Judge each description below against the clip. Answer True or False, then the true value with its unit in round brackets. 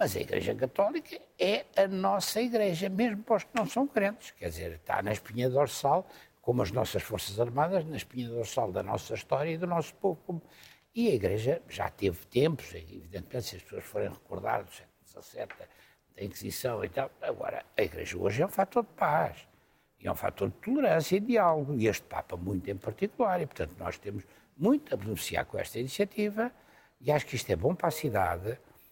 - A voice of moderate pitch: True (180 Hz)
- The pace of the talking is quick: True (205 wpm)